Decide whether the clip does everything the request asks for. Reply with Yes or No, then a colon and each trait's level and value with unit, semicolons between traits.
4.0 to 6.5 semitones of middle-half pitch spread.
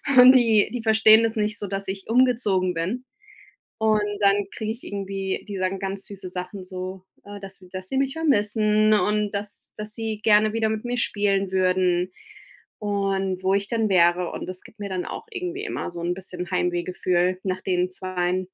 No: average, 2.7 semitones